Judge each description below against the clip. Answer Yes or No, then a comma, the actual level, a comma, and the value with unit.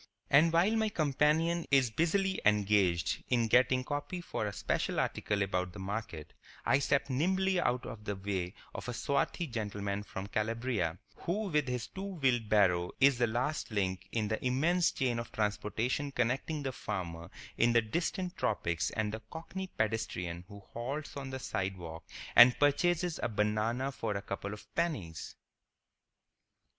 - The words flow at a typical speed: Yes, average, 160 wpm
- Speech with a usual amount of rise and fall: No, wide, 6.0 semitones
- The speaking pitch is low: Yes, low, 120 Hz